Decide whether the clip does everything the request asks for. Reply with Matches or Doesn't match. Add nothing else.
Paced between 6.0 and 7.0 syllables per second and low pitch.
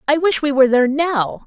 Doesn't match